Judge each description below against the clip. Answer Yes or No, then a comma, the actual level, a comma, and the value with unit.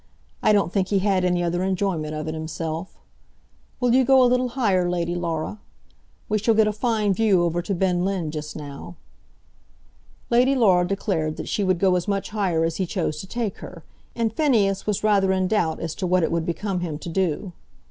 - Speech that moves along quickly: Yes, fast, 210 wpm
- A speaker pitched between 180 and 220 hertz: Yes, medium, 185 Hz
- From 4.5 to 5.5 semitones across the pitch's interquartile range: No, average, 3.7 semitones